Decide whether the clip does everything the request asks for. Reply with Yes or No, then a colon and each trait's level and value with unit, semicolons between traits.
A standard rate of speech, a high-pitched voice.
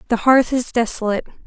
Yes: average, 165 wpm; high, 235 Hz